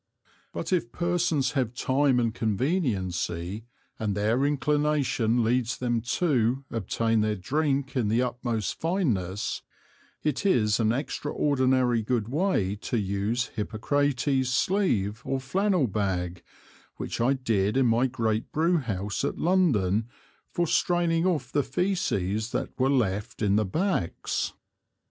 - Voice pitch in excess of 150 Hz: No, low, 125 Hz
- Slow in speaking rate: Yes, slow, 130 wpm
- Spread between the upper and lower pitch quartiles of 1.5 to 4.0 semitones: No, average, 5.2 semitones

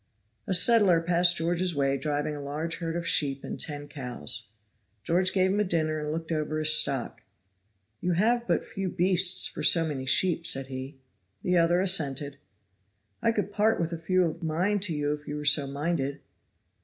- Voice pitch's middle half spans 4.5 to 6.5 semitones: No, average, 3.7 semitones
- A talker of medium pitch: Yes, medium, 165 Hz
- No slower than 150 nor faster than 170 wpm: No, average, 190 wpm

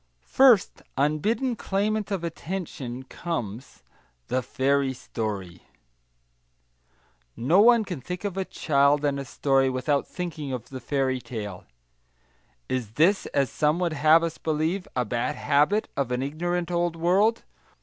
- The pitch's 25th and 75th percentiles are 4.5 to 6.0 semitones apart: Yes, wide, 5.5 semitones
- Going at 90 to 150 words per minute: Yes, average, 140 wpm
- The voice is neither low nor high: Yes, medium, 150 Hz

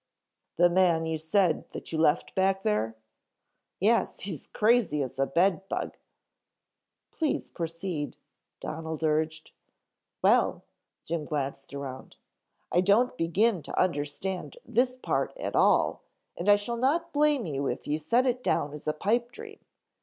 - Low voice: No, medium, 175 Hz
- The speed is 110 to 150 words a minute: Yes, average, 145 wpm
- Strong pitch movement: Yes, wide, 7.1 semitones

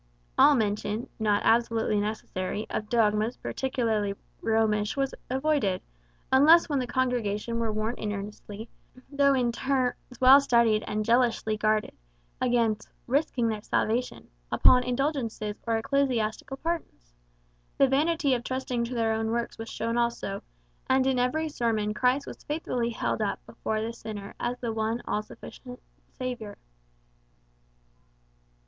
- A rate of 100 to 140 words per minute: Yes, slow, 135 wpm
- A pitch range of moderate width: Yes, average, 3.2 semitones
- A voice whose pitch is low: No, high, 235 Hz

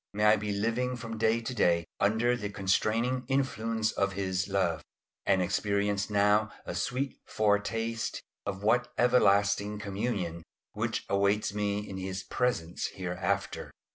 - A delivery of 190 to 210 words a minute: No, average, 140 wpm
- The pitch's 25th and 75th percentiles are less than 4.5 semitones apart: Yes, narrow, 2.6 semitones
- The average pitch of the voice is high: No, low, 105 Hz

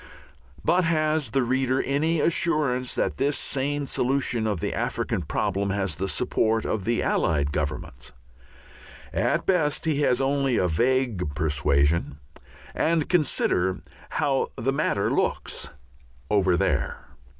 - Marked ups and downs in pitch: Yes, wide, 7.5 semitones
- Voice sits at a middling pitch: No, low, 125 Hz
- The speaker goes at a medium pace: No, slow, 130 wpm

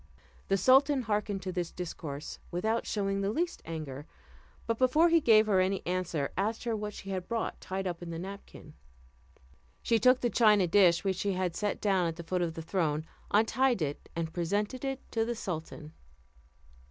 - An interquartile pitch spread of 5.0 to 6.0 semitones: No, average, 4.5 semitones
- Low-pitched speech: No, high, 195 Hz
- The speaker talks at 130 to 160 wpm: No, average, 190 wpm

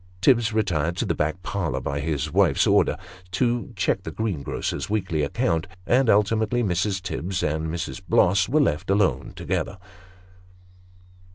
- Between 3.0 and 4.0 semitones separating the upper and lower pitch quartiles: No, average, 5.2 semitones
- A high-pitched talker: No, very low, 95 Hz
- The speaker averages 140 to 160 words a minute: Yes, average, 145 wpm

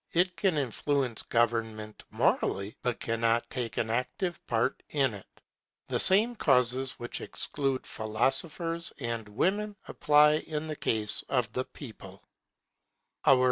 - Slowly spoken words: Yes, slow, 125 wpm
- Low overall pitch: Yes, low, 125 Hz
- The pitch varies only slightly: No, average, 5.0 semitones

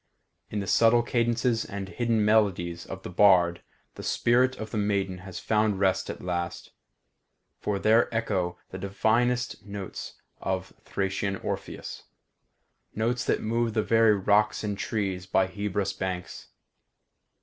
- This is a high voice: No, low, 100 Hz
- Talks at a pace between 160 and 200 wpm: No, average, 140 wpm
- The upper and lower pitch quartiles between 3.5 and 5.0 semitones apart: No, average, 3.0 semitones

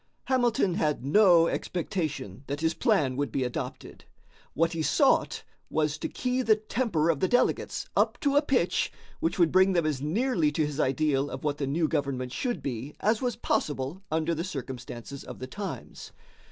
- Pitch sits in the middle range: Yes, medium, 155 Hz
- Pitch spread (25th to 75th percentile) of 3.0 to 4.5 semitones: No, wide, 5.5 semitones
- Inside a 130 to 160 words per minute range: No, average, 180 wpm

